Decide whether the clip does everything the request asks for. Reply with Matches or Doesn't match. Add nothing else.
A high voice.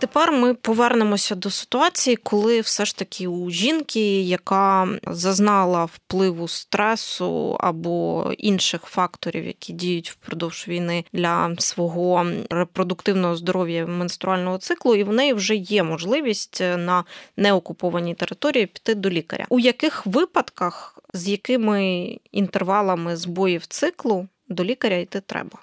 Matches